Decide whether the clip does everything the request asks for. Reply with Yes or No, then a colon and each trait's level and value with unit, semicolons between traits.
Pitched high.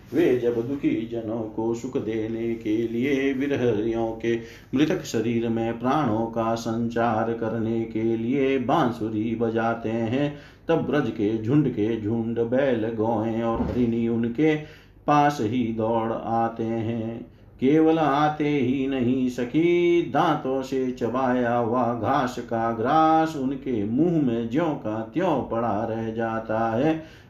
No: low, 115 Hz